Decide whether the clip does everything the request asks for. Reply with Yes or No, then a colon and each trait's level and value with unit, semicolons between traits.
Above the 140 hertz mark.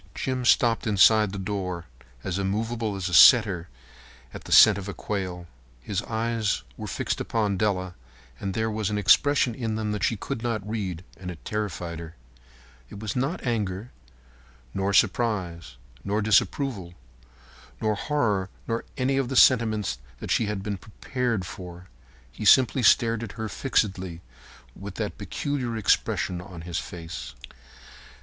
No: low, 105 Hz